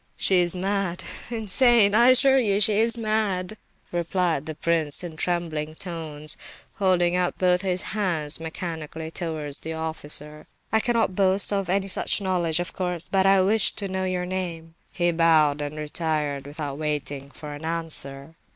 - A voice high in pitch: No, medium, 175 Hz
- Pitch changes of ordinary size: Yes, average, 3.6 semitones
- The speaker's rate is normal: Yes, average, 160 wpm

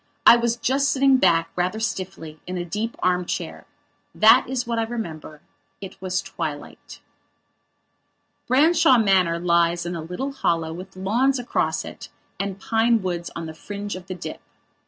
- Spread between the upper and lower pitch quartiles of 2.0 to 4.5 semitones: No, average, 5.3 semitones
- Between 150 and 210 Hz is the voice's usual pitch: Yes, high, 190 Hz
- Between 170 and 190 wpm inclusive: No, average, 160 wpm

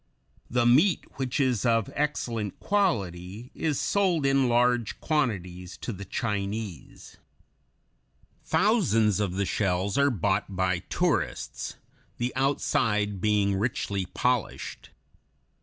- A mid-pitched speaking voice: No, low, 115 Hz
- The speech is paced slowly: Yes, slow, 110 wpm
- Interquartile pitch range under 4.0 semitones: No, average, 5.2 semitones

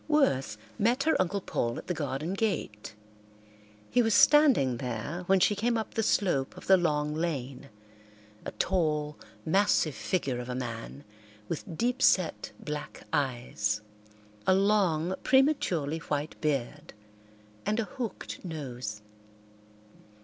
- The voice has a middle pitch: Yes, medium, 160 Hz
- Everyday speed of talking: No, slow, 130 wpm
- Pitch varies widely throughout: Yes, wide, 7.1 semitones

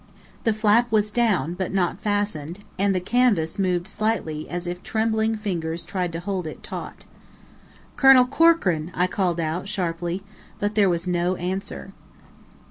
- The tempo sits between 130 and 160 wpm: Yes, average, 150 wpm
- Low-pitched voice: No, high, 190 Hz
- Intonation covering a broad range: No, average, 3.6 semitones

